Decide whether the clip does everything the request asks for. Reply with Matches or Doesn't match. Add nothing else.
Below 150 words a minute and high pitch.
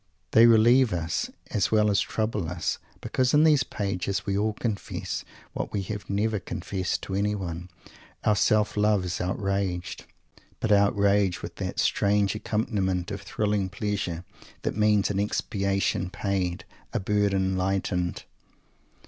Doesn't match